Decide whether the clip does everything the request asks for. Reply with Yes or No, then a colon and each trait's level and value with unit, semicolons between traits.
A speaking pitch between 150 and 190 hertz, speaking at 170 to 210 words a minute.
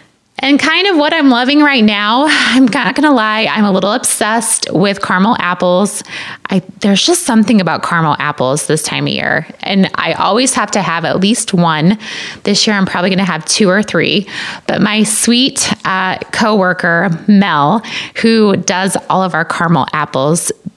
No: high, 205 Hz; average, 175 wpm